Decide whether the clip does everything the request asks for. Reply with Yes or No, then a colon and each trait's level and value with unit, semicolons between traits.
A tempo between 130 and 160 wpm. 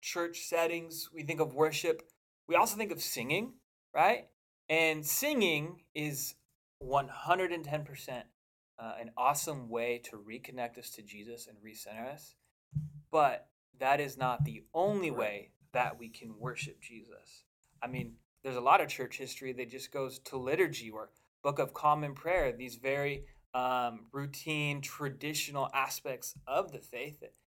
Yes: average, 150 wpm